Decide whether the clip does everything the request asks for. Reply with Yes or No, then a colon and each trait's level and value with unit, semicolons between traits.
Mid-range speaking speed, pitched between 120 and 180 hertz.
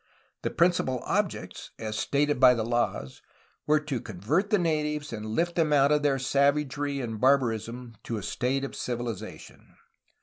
Yes: average, 160 wpm; low, 135 Hz